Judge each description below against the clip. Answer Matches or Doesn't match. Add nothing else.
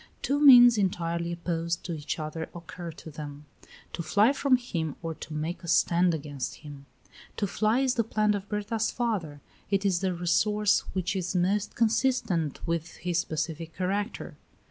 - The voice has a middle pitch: Matches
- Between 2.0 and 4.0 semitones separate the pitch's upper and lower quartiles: Doesn't match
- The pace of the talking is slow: Doesn't match